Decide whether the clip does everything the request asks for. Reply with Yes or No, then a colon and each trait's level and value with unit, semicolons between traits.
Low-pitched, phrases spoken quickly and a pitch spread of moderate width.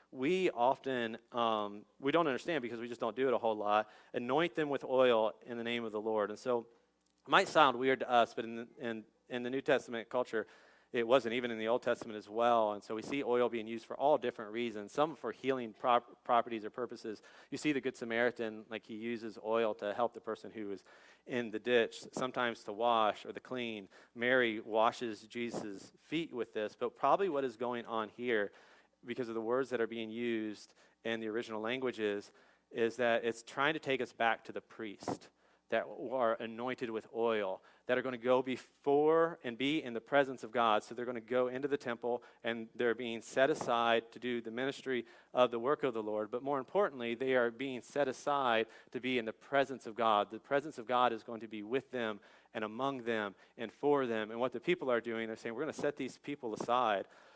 No: low, 120 Hz; fast, 225 wpm; narrow, 2.2 semitones